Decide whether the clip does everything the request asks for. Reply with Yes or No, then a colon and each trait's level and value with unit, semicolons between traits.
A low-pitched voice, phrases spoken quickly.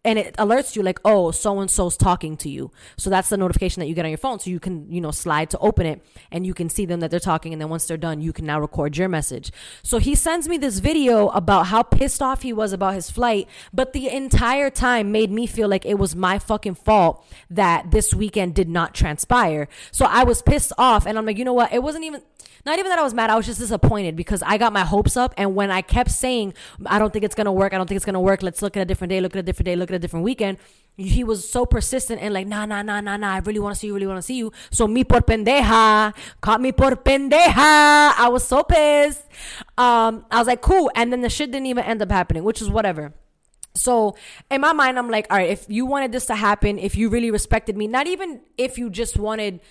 No: high, 210 Hz; fast, 270 wpm